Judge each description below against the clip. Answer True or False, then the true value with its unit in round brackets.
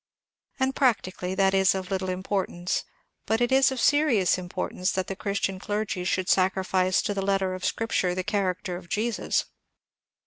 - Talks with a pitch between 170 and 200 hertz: True (190 Hz)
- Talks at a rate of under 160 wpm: False (170 wpm)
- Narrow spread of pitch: True (2.3 semitones)